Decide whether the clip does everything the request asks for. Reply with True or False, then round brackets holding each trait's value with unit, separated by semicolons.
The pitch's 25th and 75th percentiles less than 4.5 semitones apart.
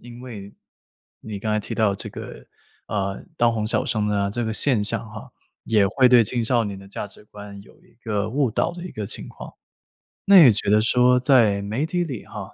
True (3.3 semitones)